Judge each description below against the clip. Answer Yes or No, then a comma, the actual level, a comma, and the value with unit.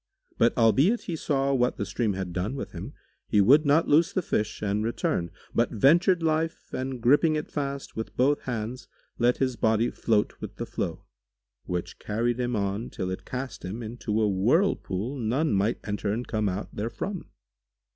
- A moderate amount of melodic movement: Yes, average, 5.0 semitones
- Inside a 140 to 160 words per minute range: No, average, 180 wpm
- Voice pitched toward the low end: Yes, low, 120 Hz